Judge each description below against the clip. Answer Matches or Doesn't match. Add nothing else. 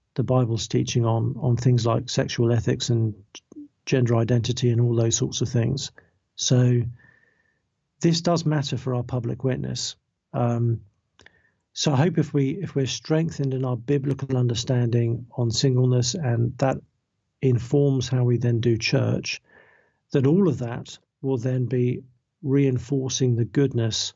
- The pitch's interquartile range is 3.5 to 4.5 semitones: Doesn't match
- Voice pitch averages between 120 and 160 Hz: Matches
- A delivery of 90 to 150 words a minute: Matches